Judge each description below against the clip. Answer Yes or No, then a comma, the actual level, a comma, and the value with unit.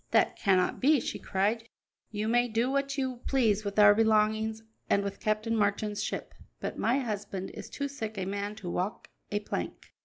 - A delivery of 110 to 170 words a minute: No, average, 185 wpm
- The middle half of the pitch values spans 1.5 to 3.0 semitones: Yes, narrow, 2.5 semitones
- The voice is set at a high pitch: Yes, high, 215 Hz